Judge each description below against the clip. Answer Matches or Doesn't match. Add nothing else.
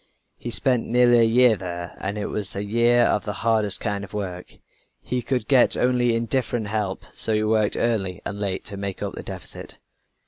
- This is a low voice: Matches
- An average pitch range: Matches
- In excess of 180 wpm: Matches